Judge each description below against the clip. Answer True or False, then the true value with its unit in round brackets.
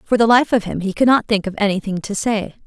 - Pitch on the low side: False (215 Hz)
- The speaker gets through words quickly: True (295 wpm)